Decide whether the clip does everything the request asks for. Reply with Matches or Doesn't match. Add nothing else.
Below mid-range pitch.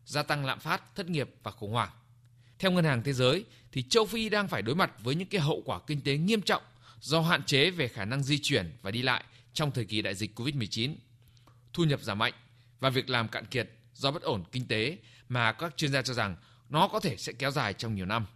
Matches